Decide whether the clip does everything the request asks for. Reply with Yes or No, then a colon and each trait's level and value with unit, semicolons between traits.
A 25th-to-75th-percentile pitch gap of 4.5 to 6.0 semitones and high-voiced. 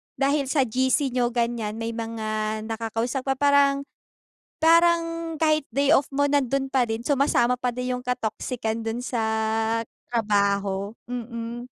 No: average, 3.6 semitones; high, 245 Hz